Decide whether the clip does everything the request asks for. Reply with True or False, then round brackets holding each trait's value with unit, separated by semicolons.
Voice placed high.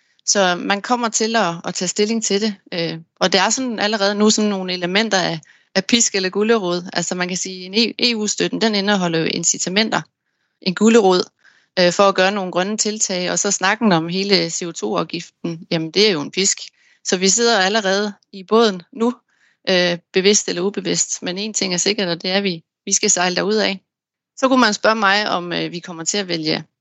True (195 Hz)